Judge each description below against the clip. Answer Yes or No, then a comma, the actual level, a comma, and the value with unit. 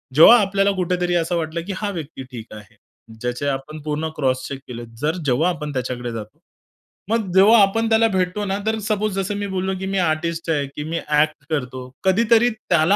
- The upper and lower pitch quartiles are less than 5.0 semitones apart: No, wide, 5.5 semitones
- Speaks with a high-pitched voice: No, medium, 170 Hz